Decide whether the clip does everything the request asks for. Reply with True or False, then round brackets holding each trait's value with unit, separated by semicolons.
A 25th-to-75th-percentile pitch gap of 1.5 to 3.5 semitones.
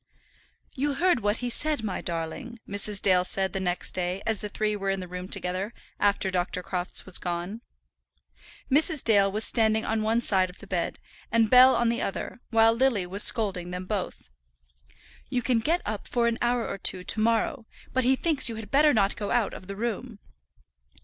False (3.9 semitones)